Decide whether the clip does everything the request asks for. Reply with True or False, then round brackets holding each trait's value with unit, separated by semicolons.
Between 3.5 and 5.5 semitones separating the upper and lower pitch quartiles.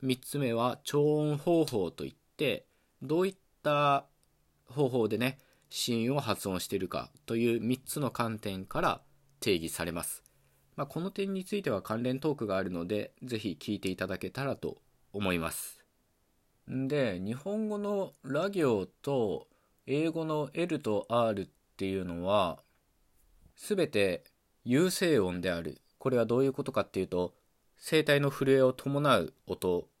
False (6.3 semitones)